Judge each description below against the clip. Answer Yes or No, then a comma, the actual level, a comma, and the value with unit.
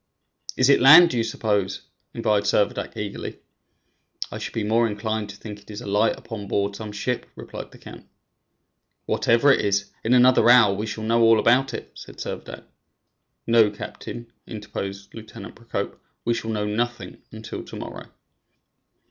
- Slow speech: No, average, 165 wpm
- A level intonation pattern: Yes, narrow, 2.2 semitones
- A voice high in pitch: No, low, 110 Hz